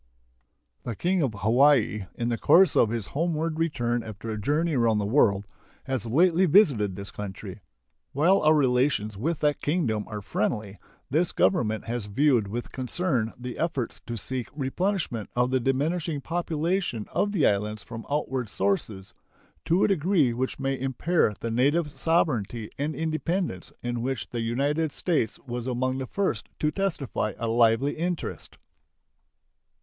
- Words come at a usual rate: Yes, average, 155 wpm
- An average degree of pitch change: No, wide, 6.0 semitones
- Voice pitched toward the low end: Yes, low, 130 Hz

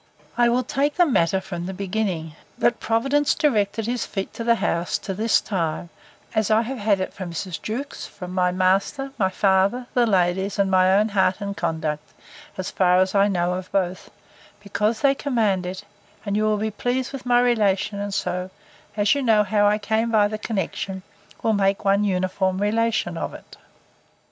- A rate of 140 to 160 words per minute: No, average, 190 wpm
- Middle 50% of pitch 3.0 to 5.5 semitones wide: Yes, average, 3.3 semitones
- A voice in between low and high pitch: No, high, 200 Hz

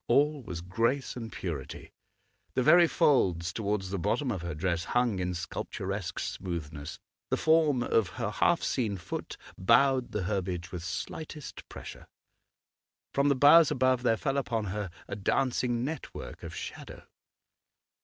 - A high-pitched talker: No, low, 110 Hz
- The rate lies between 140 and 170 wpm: Yes, average, 145 wpm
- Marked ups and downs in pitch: Yes, wide, 6.6 semitones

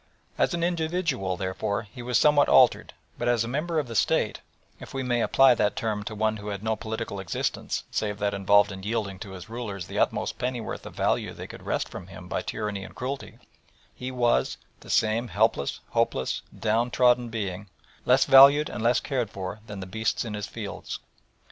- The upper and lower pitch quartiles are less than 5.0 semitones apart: Yes, average, 3.7 semitones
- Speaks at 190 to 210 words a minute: Yes, average, 195 wpm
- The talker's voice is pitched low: Yes, low, 110 Hz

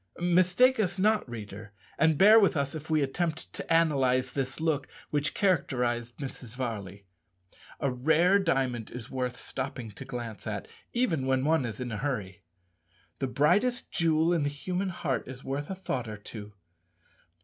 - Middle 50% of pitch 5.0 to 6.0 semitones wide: Yes, average, 5.3 semitones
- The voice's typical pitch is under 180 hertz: Yes, low, 135 Hz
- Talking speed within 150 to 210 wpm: Yes, average, 165 wpm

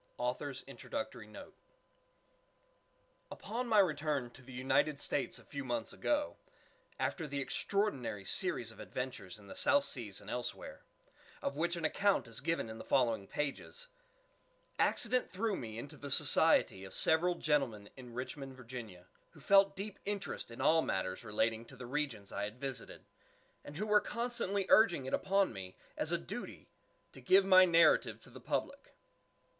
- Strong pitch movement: Yes, wide, 8.2 semitones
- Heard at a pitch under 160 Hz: Yes, medium, 140 Hz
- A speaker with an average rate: Yes, average, 165 wpm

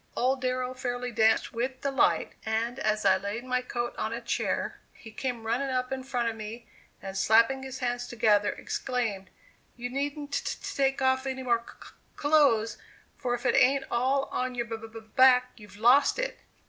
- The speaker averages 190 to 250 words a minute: Yes, average, 195 wpm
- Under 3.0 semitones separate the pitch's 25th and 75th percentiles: Yes, narrow, 2.5 semitones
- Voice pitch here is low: No, high, 245 Hz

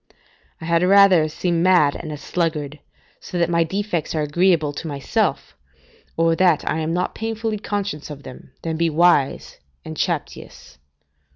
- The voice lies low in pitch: No, medium, 165 Hz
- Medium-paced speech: Yes, average, 160 wpm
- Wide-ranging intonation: No, average, 3.1 semitones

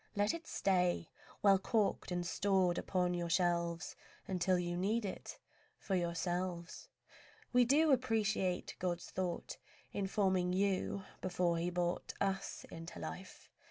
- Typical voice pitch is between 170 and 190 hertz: Yes, medium, 185 Hz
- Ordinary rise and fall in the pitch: No, narrow, 2.3 semitones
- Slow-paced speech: Yes, slow, 130 wpm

